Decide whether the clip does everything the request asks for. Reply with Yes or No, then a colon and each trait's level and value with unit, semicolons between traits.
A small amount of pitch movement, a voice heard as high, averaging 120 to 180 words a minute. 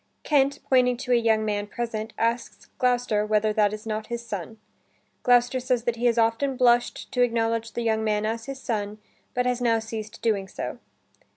No: narrow, 2.2 semitones; high, 230 Hz; average, 190 wpm